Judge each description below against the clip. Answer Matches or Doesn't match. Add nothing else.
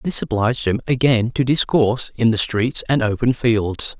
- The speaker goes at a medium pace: Matches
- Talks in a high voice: Doesn't match